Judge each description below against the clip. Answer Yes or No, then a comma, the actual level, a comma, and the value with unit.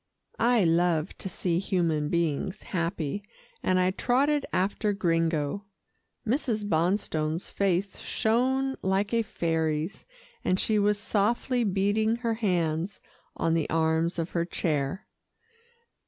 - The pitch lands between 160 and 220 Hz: Yes, medium, 185 Hz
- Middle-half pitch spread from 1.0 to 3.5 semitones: No, average, 4.4 semitones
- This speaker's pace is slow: Yes, slow, 120 wpm